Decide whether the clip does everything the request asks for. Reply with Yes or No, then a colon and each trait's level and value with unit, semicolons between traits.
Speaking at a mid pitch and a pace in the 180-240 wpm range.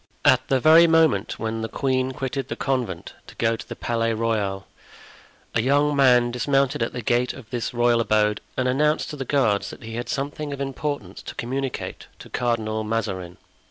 No: low, 120 Hz; average, 190 wpm